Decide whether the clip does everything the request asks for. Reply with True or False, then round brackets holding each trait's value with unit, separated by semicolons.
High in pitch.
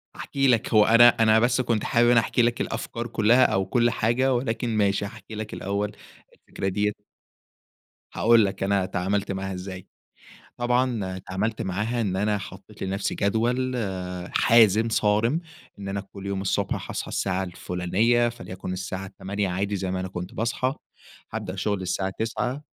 False (105 Hz)